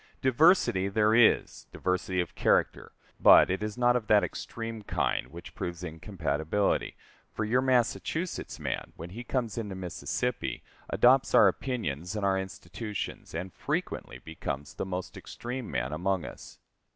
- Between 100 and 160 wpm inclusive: Yes, average, 145 wpm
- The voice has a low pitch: Yes, low, 100 Hz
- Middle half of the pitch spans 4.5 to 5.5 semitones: Yes, average, 5.1 semitones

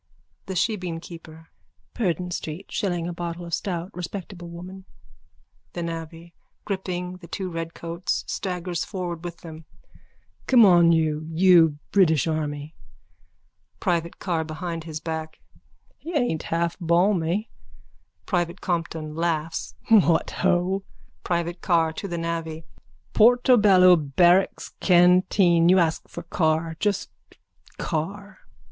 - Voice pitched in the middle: Yes, medium, 170 Hz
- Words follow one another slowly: Yes, slow, 115 wpm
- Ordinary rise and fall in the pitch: No, narrow, 2.0 semitones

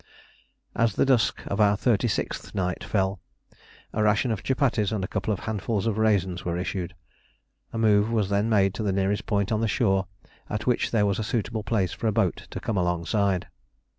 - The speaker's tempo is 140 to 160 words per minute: No, average, 200 wpm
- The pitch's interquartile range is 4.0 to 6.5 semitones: No, narrow, 2.5 semitones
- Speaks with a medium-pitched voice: No, low, 105 Hz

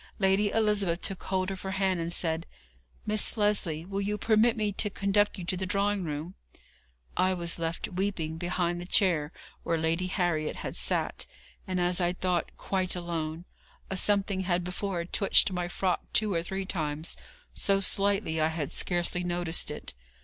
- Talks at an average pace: Yes, average, 170 wpm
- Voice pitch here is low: No, medium, 185 Hz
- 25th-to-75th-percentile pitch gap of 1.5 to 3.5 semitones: Yes, narrow, 2.6 semitones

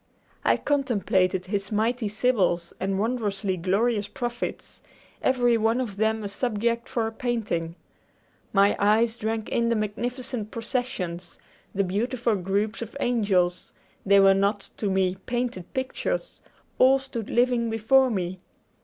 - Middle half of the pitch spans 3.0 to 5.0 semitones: Yes, average, 3.6 semitones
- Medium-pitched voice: No, high, 220 Hz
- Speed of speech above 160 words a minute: No, slow, 135 wpm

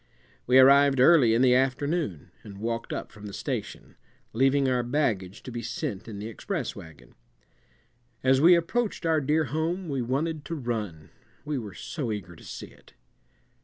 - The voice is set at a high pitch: No, low, 130 Hz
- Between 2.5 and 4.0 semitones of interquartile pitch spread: No, wide, 5.5 semitones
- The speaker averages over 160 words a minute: Yes, average, 170 wpm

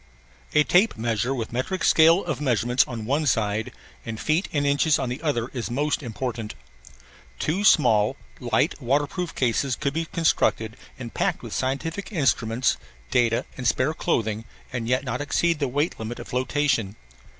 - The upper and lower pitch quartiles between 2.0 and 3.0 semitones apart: No, average, 4.4 semitones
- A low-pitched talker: Yes, low, 130 Hz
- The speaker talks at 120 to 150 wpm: No, average, 160 wpm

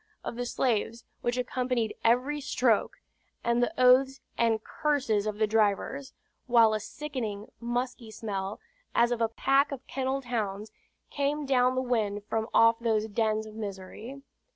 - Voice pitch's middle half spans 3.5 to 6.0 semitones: No, average, 3.1 semitones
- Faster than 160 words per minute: No, average, 150 wpm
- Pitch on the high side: Yes, high, 235 Hz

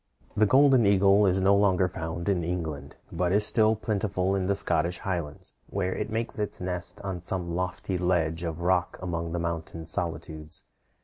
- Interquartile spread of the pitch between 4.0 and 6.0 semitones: No, average, 2.8 semitones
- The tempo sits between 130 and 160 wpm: No, average, 175 wpm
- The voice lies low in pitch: Yes, very low, 90 Hz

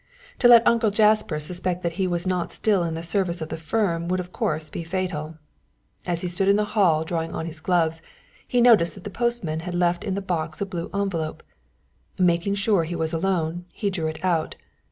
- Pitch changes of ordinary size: Yes, average, 3.2 semitones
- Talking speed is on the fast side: Yes, fast, 215 wpm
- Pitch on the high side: No, medium, 175 Hz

